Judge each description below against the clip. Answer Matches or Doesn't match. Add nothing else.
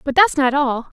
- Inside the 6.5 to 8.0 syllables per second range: Doesn't match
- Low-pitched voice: Doesn't match